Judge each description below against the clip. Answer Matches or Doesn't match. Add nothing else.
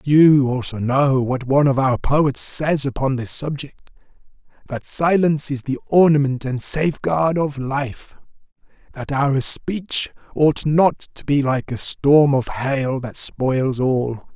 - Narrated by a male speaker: Matches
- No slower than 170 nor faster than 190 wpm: Doesn't match